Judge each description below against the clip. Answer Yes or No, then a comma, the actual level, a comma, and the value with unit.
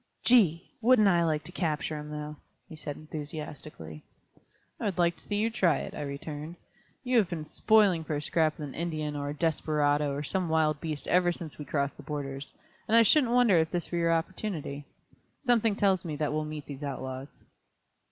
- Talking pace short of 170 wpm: No, average, 200 wpm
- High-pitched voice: No, medium, 155 Hz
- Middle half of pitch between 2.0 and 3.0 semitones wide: No, average, 3.6 semitones